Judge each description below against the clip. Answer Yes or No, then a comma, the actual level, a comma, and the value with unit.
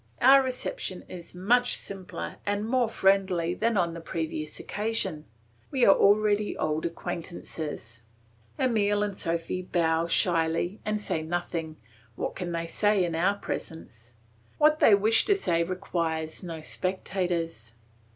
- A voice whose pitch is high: No, medium, 180 Hz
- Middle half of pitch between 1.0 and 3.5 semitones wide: No, average, 3.9 semitones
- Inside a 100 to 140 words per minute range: Yes, slow, 135 wpm